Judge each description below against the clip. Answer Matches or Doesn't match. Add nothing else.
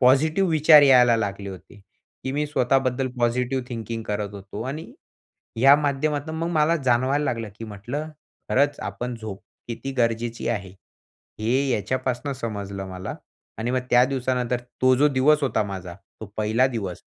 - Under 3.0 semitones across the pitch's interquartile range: Doesn't match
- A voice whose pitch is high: Doesn't match